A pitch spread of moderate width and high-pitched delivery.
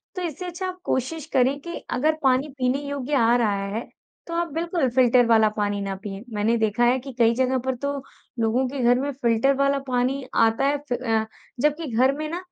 Yes: average, 3.6 semitones; very high, 260 Hz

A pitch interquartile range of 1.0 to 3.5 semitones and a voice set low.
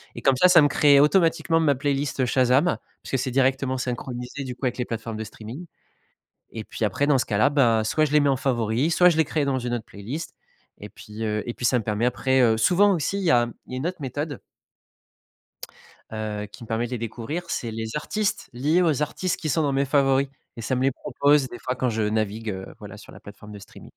No: average, 4.3 semitones; low, 130 Hz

